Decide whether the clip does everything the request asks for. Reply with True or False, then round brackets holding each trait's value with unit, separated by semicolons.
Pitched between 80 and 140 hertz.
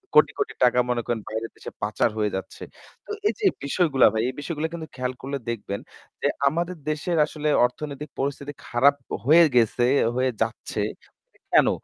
True (135 Hz)